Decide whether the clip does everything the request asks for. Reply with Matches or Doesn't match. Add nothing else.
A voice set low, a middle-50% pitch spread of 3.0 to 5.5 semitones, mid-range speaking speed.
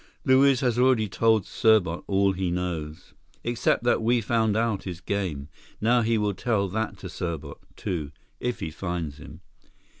Matches